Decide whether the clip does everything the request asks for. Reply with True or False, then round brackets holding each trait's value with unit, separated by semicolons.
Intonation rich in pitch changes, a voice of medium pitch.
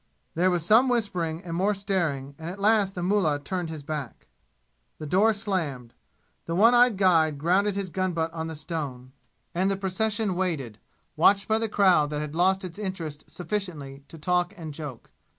False (4.2 semitones; 180 Hz)